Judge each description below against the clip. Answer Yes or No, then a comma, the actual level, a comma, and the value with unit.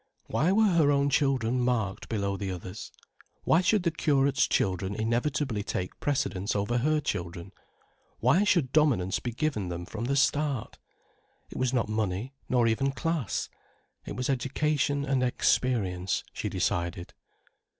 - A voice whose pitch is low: Yes, low, 125 Hz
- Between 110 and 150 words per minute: Yes, average, 145 wpm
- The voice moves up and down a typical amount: No, wide, 6.1 semitones